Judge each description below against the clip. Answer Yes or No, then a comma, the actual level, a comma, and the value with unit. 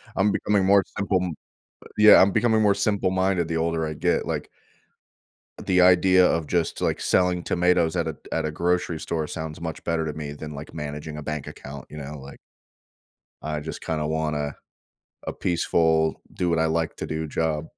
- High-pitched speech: No, very low, 80 Hz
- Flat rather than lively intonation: No, average, 3.0 semitones